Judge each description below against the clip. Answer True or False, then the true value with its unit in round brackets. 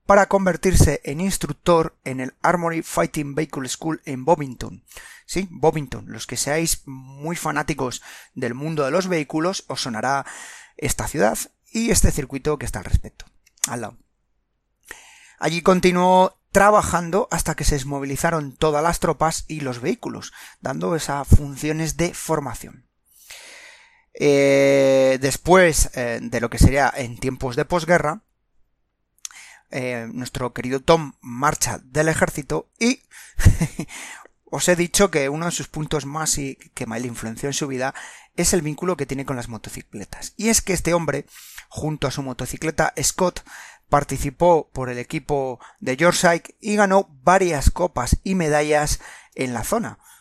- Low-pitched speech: False (150 Hz)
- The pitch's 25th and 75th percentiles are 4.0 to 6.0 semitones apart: True (4.3 semitones)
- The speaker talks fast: False (150 wpm)